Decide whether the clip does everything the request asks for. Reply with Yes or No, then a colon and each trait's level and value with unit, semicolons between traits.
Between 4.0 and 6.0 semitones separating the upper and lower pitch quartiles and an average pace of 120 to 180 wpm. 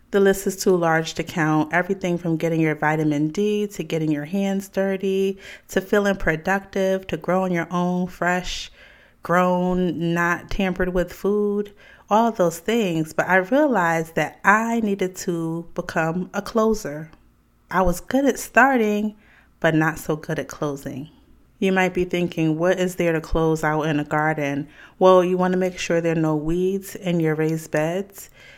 No: average, 3.3 semitones; average, 170 wpm